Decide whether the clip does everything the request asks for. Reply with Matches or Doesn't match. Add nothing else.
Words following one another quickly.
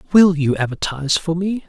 Doesn't match